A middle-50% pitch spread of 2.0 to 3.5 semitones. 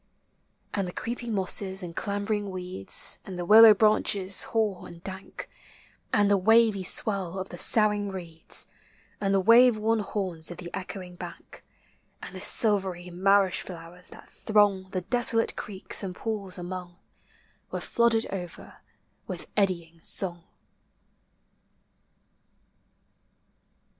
Yes: average, 2.7 semitones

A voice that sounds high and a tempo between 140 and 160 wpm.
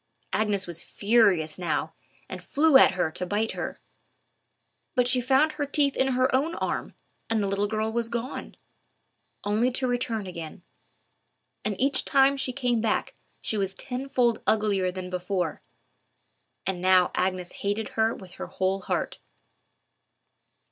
Yes: high, 220 Hz; average, 145 wpm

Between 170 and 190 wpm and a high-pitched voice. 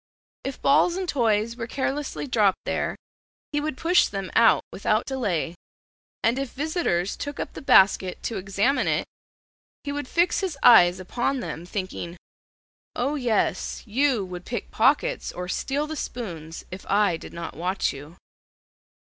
No: average, 155 wpm; high, 230 Hz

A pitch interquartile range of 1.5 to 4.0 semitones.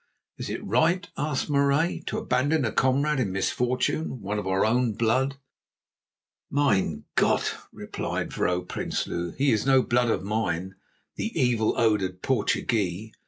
No: average, 5.2 semitones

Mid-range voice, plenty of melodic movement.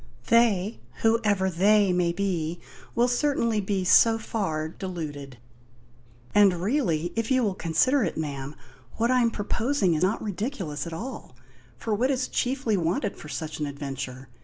No: high, 195 Hz; wide, 6.0 semitones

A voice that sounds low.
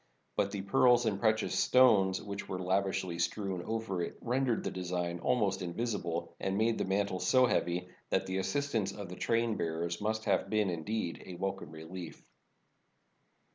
Yes: very low, 95 Hz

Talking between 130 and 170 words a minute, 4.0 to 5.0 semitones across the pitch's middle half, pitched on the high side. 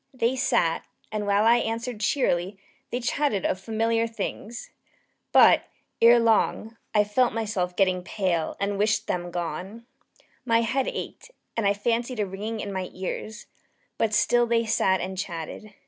No: average, 160 wpm; average, 3.3 semitones; high, 215 Hz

